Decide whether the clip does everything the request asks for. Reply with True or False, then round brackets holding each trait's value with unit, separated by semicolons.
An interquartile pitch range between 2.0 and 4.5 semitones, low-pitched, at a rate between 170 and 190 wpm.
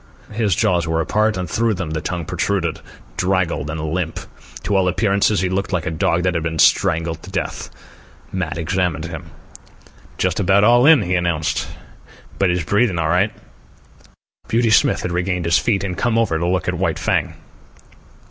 True (3.2 semitones; 90 Hz; 180 wpm)